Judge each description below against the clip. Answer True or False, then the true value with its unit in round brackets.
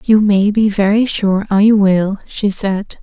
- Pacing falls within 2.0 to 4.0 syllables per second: True (3.6 syllables/s)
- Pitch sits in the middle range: False (205 Hz)